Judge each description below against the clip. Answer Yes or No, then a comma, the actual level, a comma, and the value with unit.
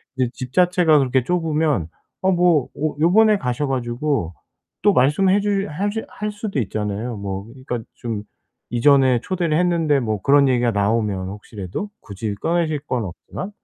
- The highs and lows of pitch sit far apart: Yes, wide, 7.1 semitones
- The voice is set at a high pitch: No, medium, 140 Hz